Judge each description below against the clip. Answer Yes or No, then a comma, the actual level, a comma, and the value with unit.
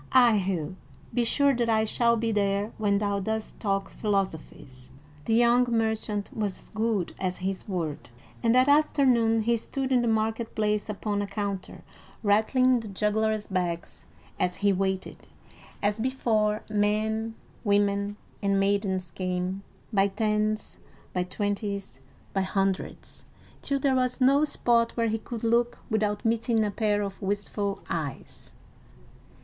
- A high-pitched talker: Yes, high, 210 Hz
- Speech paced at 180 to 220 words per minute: No, average, 145 wpm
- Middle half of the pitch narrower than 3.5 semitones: Yes, narrow, 2.6 semitones